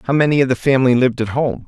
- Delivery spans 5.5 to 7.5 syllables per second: Yes, 7.4 syllables/s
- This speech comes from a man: Yes, male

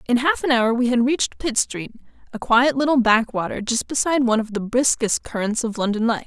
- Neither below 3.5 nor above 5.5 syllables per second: No, 5.8 syllables/s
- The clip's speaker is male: No, female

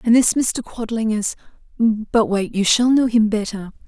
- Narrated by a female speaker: Yes, female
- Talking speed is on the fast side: No, average, 170 wpm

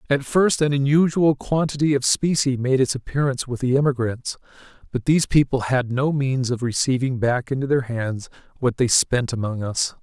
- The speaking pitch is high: No, low, 130 Hz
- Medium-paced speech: Yes, average, 180 wpm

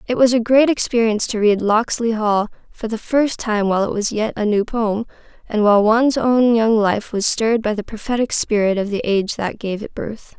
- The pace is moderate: No, fast, 225 wpm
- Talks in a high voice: Yes, high, 220 Hz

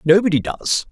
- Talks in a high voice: No, medium, 155 Hz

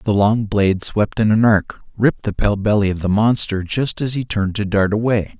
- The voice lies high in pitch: No, low, 105 Hz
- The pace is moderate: No, fast, 235 wpm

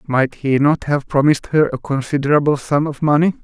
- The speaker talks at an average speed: Yes, average, 190 wpm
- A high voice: No, medium, 145 Hz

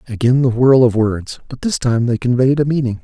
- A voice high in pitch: No, low, 125 Hz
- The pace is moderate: No, fast, 235 wpm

